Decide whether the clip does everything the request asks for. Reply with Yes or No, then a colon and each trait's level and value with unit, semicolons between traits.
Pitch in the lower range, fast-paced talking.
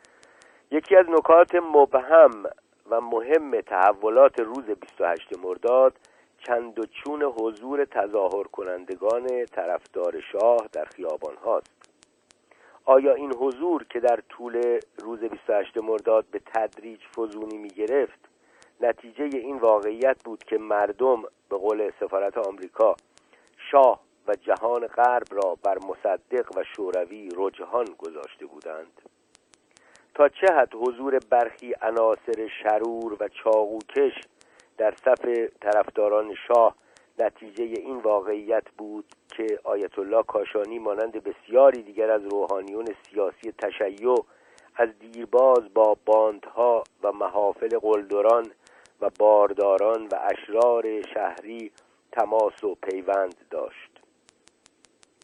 No: low, 130 Hz; average, 110 wpm